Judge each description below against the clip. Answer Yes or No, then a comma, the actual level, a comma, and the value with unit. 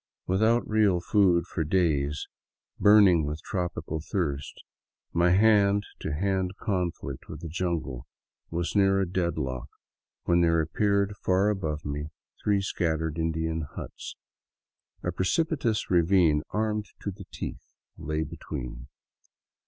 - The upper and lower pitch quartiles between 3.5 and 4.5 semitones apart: Yes, average, 4.0 semitones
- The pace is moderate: No, slow, 125 wpm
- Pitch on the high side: No, very low, 85 Hz